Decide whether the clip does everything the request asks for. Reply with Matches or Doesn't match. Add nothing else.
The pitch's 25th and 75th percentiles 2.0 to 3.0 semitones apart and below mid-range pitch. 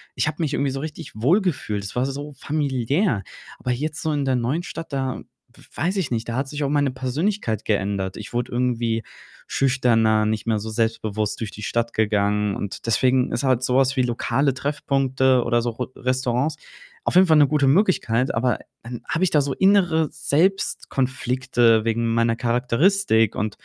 Doesn't match